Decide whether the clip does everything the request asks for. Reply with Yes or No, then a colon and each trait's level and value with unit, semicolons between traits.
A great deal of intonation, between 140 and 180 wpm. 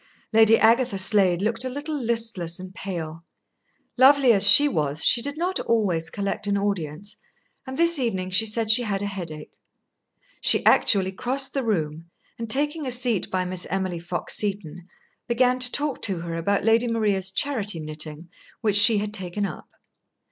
No: average, 4.8 semitones; average, 170 wpm